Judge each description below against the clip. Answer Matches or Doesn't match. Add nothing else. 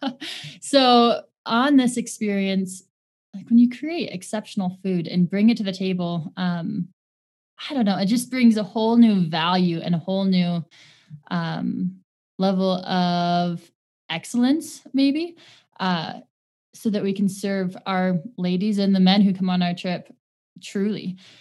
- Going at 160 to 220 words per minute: Doesn't match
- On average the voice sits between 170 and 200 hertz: Matches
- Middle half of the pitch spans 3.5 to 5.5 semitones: Matches